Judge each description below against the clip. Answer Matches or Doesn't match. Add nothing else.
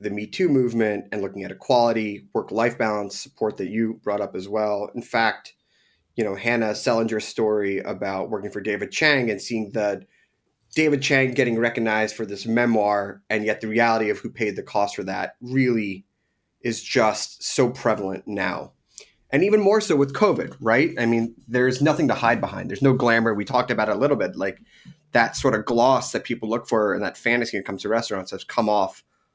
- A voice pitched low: Matches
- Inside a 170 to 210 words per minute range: Matches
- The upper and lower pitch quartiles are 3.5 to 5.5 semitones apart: Doesn't match